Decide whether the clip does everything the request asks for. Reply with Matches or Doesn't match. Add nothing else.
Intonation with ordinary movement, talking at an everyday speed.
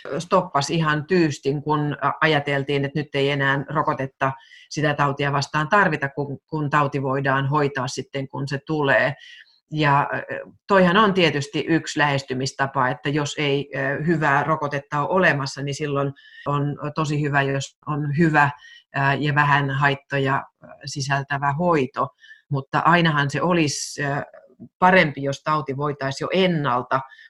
Doesn't match